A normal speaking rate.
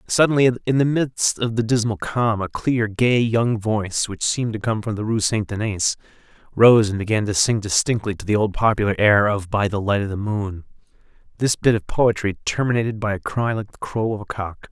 No: fast, 220 wpm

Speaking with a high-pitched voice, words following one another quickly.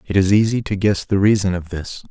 No: low, 100 Hz; fast, 255 wpm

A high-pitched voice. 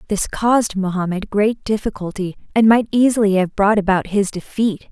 Yes: high, 205 Hz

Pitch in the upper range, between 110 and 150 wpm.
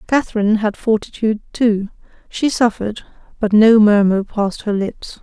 Yes: high, 215 Hz; average, 140 wpm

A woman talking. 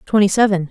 Yes: female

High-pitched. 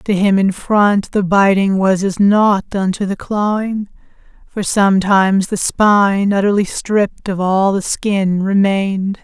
Yes: high, 195 Hz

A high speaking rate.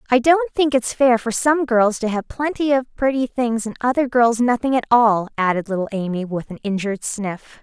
Yes: fast, 210 wpm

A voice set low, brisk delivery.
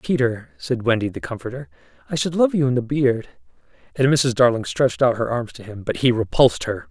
Yes: low, 120 Hz; fast, 215 wpm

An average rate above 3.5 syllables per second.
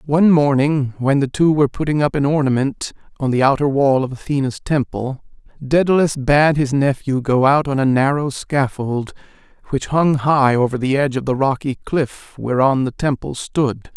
Yes: 4.9 syllables/s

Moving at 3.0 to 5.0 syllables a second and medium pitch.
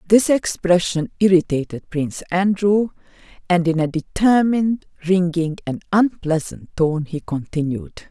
Yes: 4.5 syllables/s; medium, 175 Hz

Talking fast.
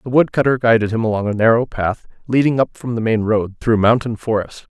Yes: fast, 215 wpm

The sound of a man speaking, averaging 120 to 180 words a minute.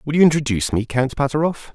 No: male; fast, 205 wpm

